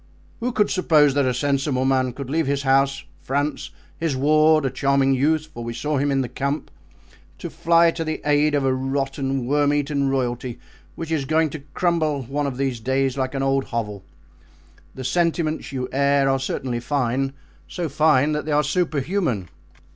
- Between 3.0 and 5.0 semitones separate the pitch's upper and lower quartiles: No, narrow, 2.5 semitones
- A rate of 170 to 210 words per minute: Yes, average, 175 wpm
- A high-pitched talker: No, medium, 140 Hz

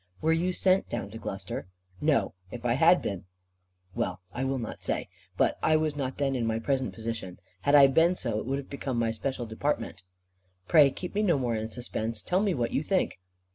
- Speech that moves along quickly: Yes, fast, 215 wpm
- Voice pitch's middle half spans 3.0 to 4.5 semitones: No, average, 5.3 semitones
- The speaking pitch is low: Yes, low, 130 Hz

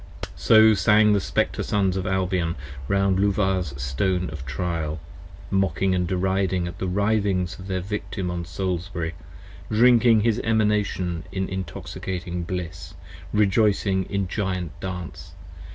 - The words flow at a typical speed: No, slow, 125 wpm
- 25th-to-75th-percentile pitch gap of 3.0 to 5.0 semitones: No, narrow, 2.4 semitones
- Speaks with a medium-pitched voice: No, very low, 95 Hz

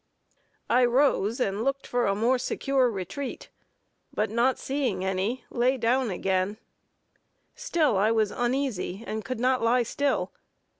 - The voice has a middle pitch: No, high, 240 Hz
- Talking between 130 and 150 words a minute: Yes, average, 140 wpm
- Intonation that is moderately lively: Yes, average, 3.9 semitones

